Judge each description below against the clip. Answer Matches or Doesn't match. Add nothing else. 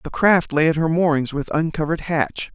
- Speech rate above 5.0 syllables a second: Matches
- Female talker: Doesn't match